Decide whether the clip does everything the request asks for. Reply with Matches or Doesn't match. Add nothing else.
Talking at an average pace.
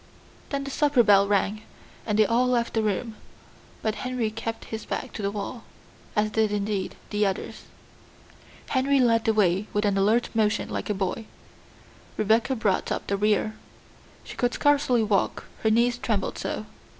Matches